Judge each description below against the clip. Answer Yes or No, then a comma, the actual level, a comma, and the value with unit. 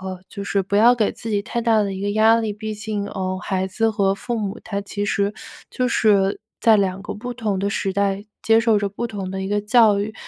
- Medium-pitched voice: No, high, 205 Hz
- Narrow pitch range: Yes, narrow, 2.1 semitones